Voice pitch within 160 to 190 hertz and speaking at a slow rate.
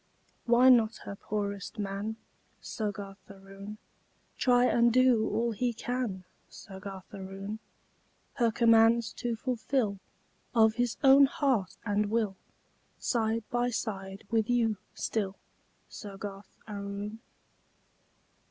No: high, 220 Hz; slow, 105 wpm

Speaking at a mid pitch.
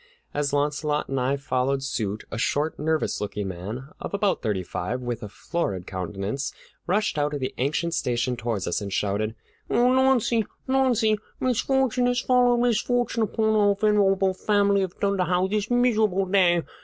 Yes: medium, 170 Hz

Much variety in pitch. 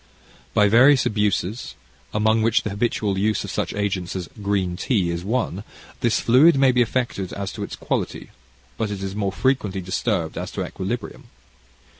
No: average, 3.4 semitones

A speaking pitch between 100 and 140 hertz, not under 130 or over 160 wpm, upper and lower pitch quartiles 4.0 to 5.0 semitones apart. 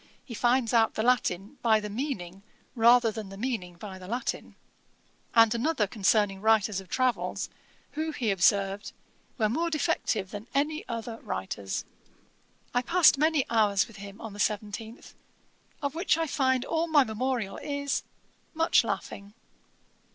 No: high, 225 Hz; average, 150 wpm; average, 4.6 semitones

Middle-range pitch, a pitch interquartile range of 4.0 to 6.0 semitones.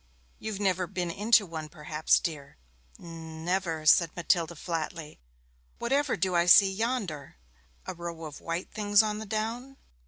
Yes: medium, 175 Hz; average, 4.3 semitones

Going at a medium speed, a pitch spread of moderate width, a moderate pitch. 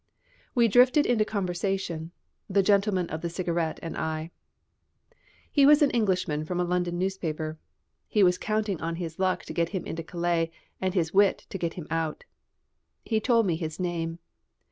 Yes: average, 170 wpm; average, 3.3 semitones; medium, 180 Hz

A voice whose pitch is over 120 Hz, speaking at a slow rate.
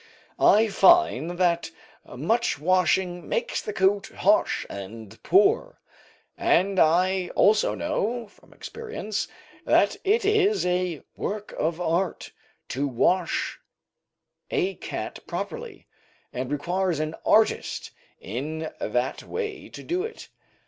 Yes: medium, 185 Hz; slow, 115 wpm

